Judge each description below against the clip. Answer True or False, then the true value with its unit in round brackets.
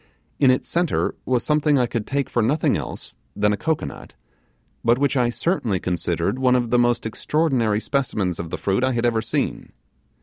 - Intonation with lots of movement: False (3.9 semitones)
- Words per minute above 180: True (190 wpm)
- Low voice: True (120 Hz)